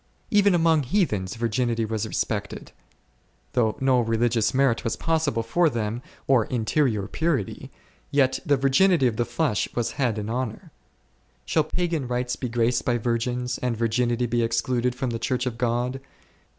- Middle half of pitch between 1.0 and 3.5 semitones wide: Yes, average, 2.8 semitones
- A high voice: No, low, 125 Hz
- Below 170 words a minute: Yes, average, 155 wpm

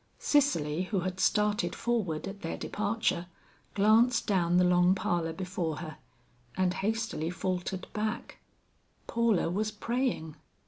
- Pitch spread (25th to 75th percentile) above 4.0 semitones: No, average, 3.7 semitones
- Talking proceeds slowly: Yes, slow, 125 wpm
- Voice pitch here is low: No, high, 190 Hz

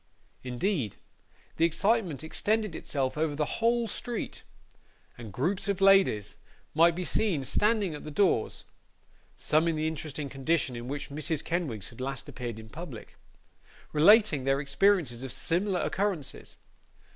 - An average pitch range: No, wide, 6.3 semitones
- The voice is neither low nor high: Yes, medium, 155 Hz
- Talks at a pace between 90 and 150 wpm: Yes, average, 140 wpm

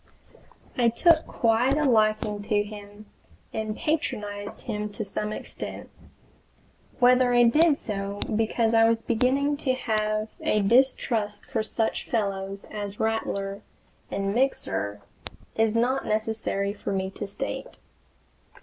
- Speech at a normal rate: No, slow, 125 wpm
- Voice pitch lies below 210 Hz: No, high, 215 Hz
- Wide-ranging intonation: No, average, 2.9 semitones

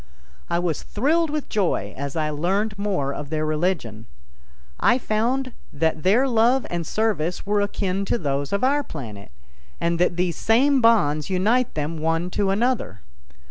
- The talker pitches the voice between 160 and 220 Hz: Yes, medium, 185 Hz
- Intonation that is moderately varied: No, wide, 6.6 semitones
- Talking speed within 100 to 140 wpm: No, average, 160 wpm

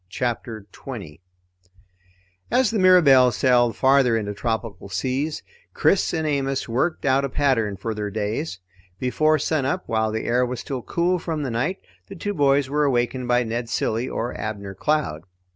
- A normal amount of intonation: Yes, average, 4.8 semitones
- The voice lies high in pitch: No, low, 125 Hz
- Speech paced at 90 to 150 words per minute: No, average, 160 wpm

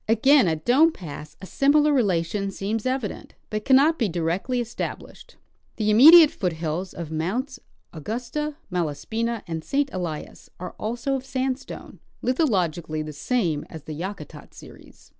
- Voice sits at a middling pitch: No, high, 215 Hz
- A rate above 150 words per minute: No, average, 140 wpm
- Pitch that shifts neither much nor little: No, wide, 7.7 semitones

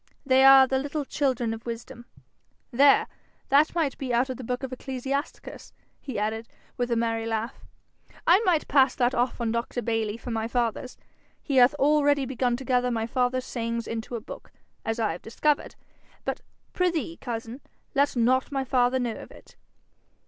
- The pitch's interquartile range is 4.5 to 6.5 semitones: No, average, 2.7 semitones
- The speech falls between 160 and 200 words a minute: Yes, average, 180 wpm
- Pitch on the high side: Yes, very high, 250 Hz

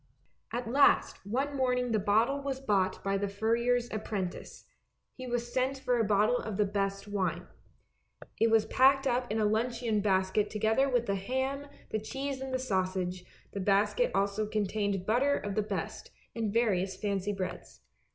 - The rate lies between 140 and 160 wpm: No, average, 170 wpm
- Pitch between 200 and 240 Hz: Yes, high, 220 Hz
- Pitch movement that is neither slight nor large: Yes, average, 3.9 semitones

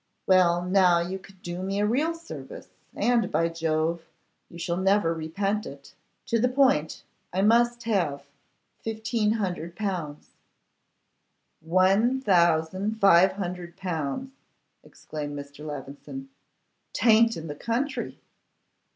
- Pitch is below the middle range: No, medium, 185 Hz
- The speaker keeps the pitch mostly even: No, average, 5.1 semitones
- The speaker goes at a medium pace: No, slow, 115 wpm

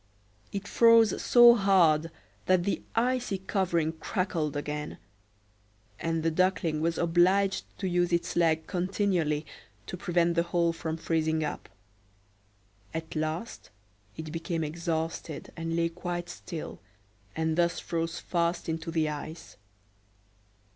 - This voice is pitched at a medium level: Yes, medium, 170 Hz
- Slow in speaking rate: Yes, slow, 125 wpm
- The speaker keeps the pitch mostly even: Yes, narrow, 2.3 semitones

